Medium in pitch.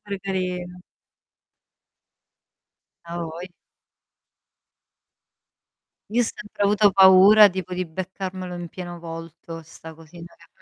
Yes: medium, 180 Hz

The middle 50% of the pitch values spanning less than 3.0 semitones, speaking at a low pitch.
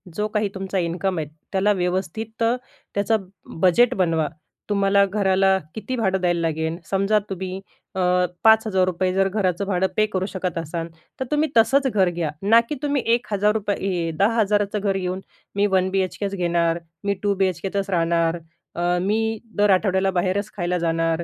No: narrow, 2.6 semitones; high, 190 Hz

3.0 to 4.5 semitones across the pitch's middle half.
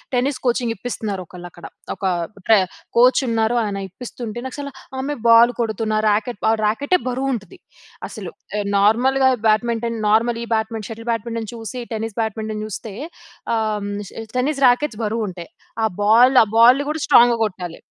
No: narrow, 2.4 semitones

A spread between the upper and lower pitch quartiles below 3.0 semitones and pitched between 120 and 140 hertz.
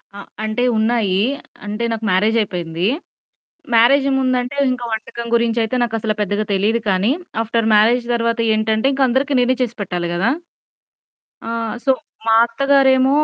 No: narrow, 2.5 semitones; high, 230 Hz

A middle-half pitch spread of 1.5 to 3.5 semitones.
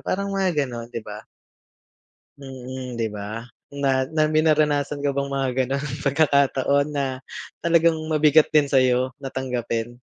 Yes: average, 3.0 semitones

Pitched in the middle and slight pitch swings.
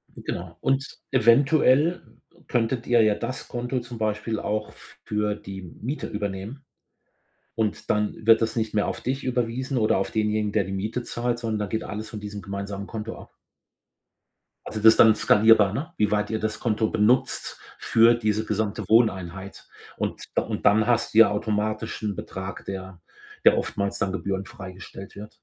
No: low, 110 Hz; narrow, 2.3 semitones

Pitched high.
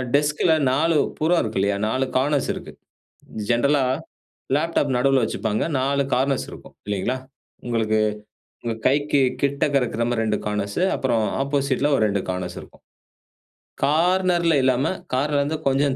No: low, 135 Hz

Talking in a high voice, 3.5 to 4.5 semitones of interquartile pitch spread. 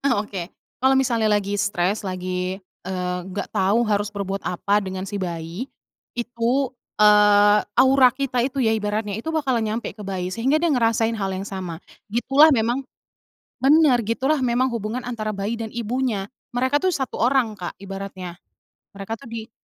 Yes: high, 220 Hz; average, 4.2 semitones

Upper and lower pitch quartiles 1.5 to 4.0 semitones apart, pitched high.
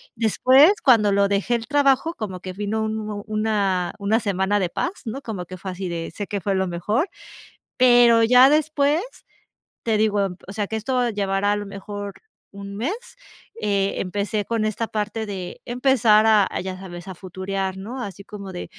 Yes: average, 2.9 semitones; high, 205 Hz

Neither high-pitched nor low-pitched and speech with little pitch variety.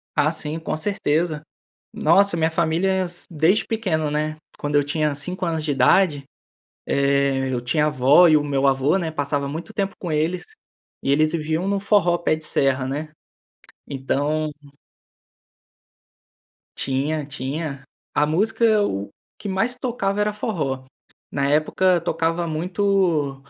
No: medium, 155 Hz; average, 3.9 semitones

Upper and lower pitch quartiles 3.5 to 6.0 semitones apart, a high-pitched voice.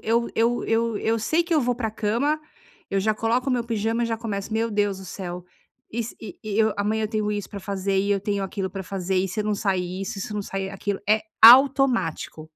No: average, 2.8 semitones; high, 210 Hz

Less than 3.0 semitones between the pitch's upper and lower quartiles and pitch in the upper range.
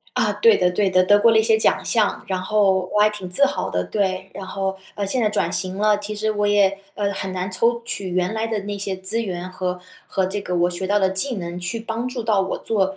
Yes: narrow, 2.5 semitones; high, 200 Hz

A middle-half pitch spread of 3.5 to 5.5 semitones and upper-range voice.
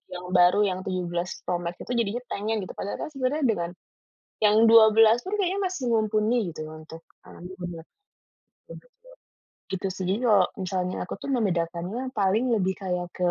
Yes: average, 4.2 semitones; high, 195 Hz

